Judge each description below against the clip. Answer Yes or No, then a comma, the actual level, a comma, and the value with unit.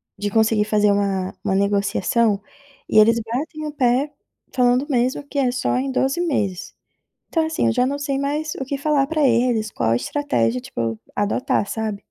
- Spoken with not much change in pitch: No, wide, 5.6 semitones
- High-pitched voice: Yes, high, 240 Hz